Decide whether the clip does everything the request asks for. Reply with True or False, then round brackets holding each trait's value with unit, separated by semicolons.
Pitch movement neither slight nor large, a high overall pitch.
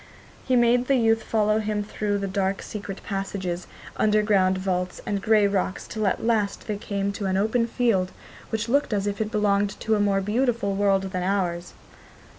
False (2.1 semitones; 205 Hz)